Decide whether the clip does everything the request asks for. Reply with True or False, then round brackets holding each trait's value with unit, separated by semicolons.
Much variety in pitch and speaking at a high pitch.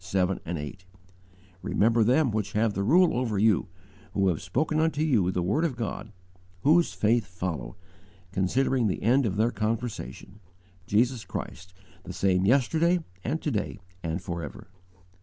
False (5.7 semitones; 110 Hz)